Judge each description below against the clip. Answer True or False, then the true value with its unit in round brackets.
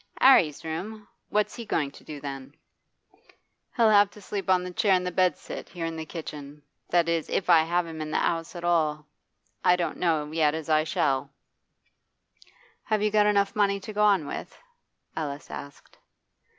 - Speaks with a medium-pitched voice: True (170 Hz)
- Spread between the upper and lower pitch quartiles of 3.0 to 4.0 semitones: False (4.6 semitones)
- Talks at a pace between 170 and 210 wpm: True (180 wpm)